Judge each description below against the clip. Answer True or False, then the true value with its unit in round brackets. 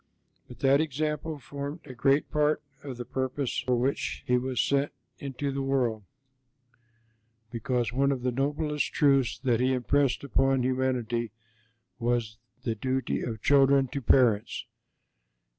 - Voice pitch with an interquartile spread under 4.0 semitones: True (2.4 semitones)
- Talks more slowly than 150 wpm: True (140 wpm)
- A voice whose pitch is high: False (130 Hz)